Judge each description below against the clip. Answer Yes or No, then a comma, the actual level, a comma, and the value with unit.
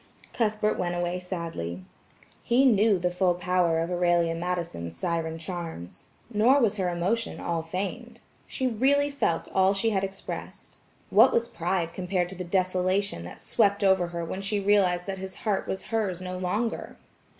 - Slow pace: No, average, 165 wpm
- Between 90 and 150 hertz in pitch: No, medium, 185 Hz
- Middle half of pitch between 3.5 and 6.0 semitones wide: No, average, 2.8 semitones